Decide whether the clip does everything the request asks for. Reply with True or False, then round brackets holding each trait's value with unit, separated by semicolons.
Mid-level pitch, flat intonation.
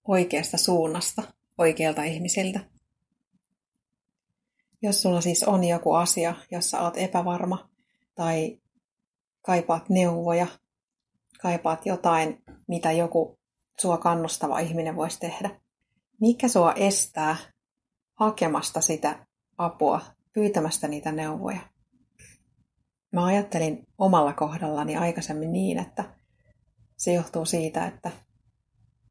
False (170 Hz; 3.3 semitones)